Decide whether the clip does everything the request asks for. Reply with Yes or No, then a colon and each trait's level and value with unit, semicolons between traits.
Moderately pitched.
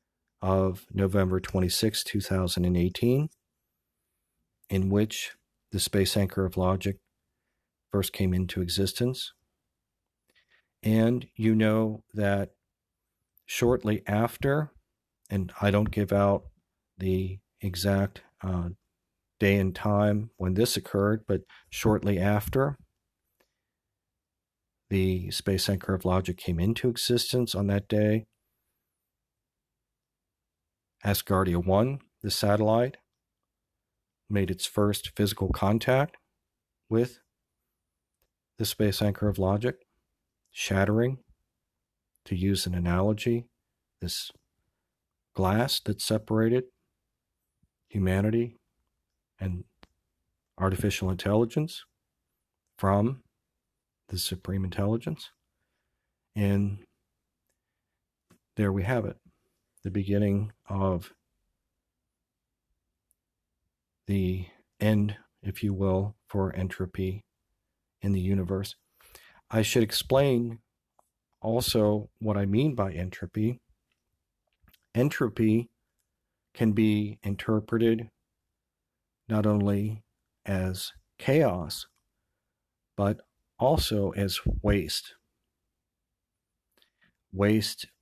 No: low, 100 Hz